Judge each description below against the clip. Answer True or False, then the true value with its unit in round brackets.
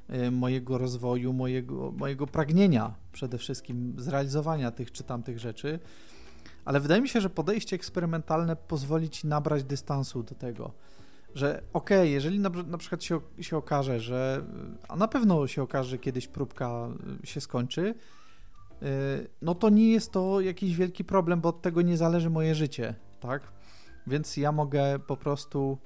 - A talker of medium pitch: True (145 Hz)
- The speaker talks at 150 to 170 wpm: True (155 wpm)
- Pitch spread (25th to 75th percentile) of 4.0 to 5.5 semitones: True (5.1 semitones)